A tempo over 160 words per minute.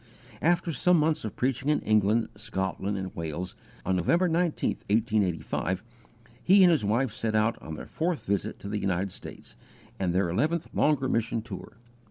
Yes: average, 170 wpm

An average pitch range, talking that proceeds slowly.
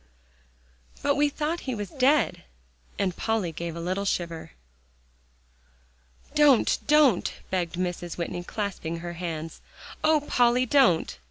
No: wide, 8.0 semitones; slow, 120 wpm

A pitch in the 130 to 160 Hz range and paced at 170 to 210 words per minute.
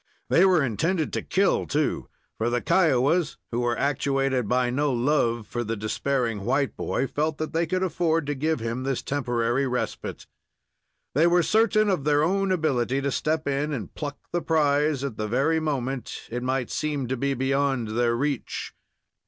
Yes: medium, 140 Hz; average, 175 wpm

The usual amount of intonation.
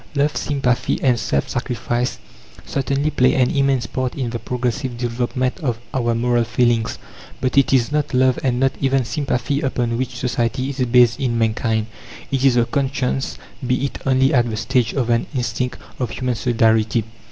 No: narrow, 2.0 semitones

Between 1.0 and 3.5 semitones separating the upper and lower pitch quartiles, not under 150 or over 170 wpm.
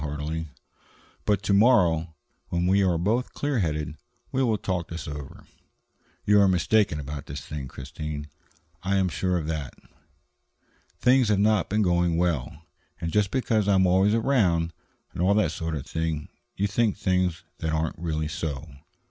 No: average, 4.4 semitones; average, 165 wpm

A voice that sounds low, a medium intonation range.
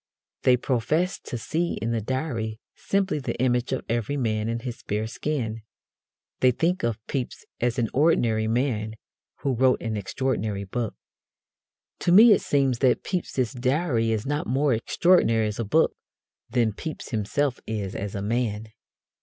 Yes: low, 120 Hz; average, 4.0 semitones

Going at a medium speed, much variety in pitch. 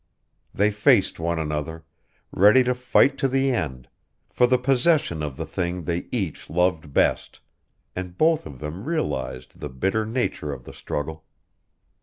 Yes: average, 155 wpm; wide, 8.6 semitones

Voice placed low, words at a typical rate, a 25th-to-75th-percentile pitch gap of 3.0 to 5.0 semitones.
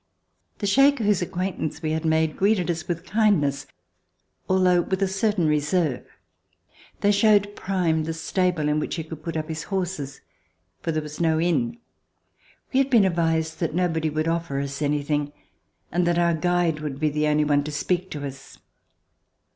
No: medium, 165 Hz; average, 180 wpm; average, 3.5 semitones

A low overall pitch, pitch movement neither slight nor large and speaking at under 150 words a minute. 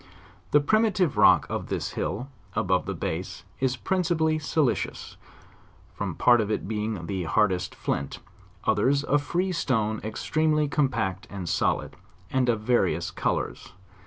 No: low, 125 Hz; wide, 6.8 semitones; average, 140 wpm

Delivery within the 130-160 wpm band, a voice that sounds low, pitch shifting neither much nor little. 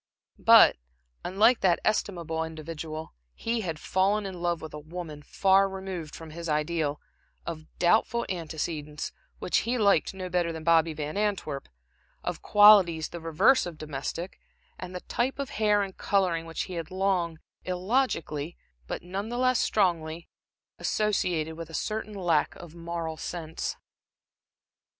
No: average, 145 wpm; medium, 175 Hz; average, 3.5 semitones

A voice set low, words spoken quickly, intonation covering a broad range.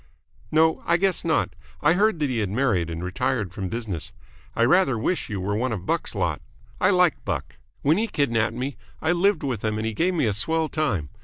Yes: low, 130 Hz; fast, 220 wpm; wide, 7.4 semitones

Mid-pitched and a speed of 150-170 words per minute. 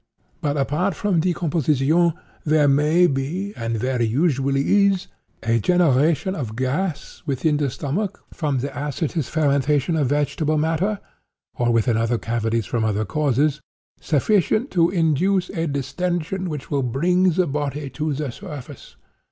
No: medium, 150 Hz; average, 140 wpm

